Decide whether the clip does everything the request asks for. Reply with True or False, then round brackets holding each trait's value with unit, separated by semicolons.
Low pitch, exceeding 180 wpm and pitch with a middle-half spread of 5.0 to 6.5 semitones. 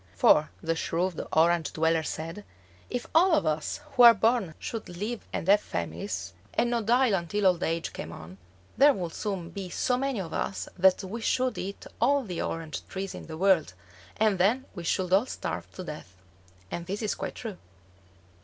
False (190 Hz; 190 wpm; 5.5 semitones)